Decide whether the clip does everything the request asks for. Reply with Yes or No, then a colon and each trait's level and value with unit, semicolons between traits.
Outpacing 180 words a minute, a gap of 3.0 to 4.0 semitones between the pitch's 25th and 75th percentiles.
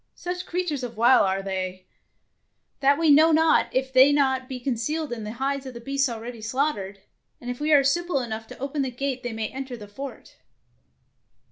Yes: fast, 205 wpm; average, 3.6 semitones